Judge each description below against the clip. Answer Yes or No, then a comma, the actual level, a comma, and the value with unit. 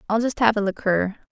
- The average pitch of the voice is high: Yes, high, 215 Hz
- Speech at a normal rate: No, fast, 230 wpm